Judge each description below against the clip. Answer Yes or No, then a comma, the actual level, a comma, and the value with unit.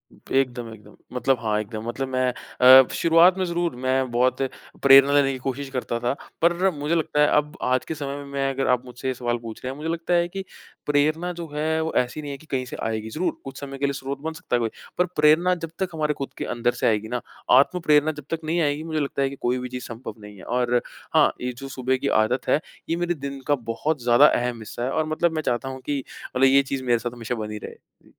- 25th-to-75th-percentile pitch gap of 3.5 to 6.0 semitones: Yes, average, 3.8 semitones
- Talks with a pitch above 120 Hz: Yes, low, 135 Hz